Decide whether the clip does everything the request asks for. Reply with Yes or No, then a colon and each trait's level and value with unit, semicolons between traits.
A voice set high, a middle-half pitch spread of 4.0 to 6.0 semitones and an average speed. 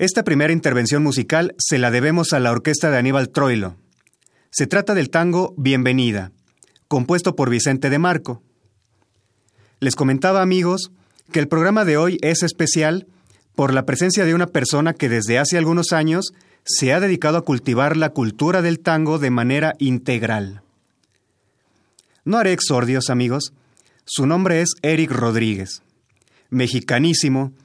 No: medium, 140 Hz; average, 5.2 semitones; average, 145 wpm